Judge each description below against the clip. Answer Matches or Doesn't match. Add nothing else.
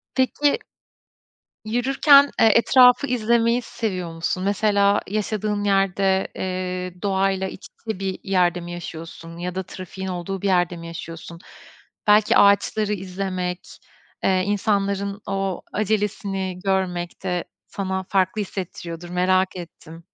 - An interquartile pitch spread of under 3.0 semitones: Matches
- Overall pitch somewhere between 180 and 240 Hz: Matches